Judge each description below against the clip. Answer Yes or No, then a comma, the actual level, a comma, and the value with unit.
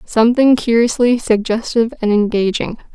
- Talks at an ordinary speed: No, slow, 100 wpm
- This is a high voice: Yes, high, 225 Hz